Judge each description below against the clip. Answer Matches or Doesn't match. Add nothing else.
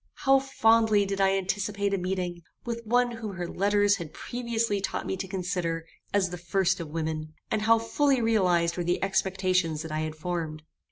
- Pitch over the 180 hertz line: Matches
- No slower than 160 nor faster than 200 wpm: Matches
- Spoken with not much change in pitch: Doesn't match